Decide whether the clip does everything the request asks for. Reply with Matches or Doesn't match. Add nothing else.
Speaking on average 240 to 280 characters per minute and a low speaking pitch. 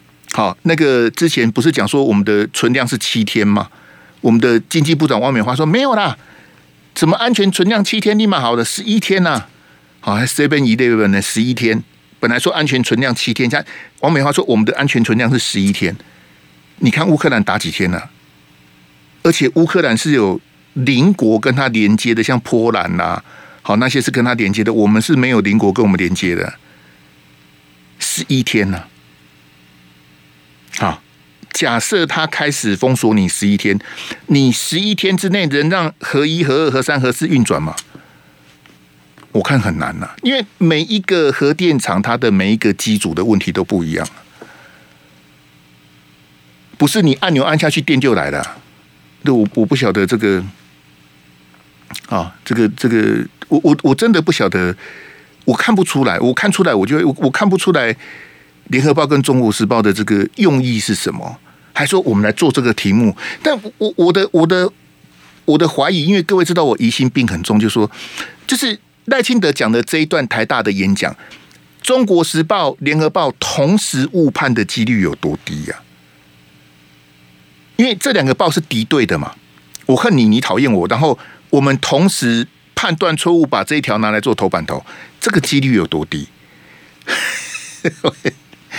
Matches